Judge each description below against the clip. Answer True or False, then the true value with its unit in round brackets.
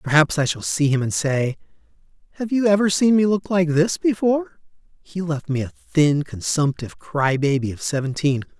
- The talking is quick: False (180 wpm)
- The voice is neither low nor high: True (160 Hz)